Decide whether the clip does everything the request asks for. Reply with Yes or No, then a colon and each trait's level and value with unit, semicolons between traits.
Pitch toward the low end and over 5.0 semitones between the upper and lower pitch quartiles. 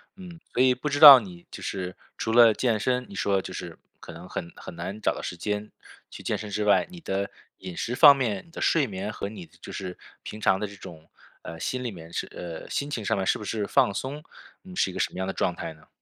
Yes: low, 105 Hz; wide, 5.4 semitones